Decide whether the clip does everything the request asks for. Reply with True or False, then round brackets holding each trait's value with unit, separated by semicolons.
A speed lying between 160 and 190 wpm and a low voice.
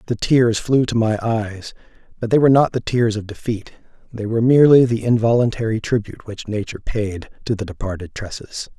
True (185 wpm; 115 Hz)